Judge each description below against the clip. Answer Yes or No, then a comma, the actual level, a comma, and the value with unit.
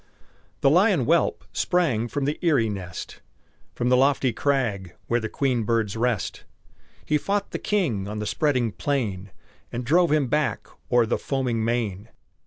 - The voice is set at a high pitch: No, low, 120 Hz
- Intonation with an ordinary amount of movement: Yes, average, 4.6 semitones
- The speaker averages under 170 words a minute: Yes, average, 160 wpm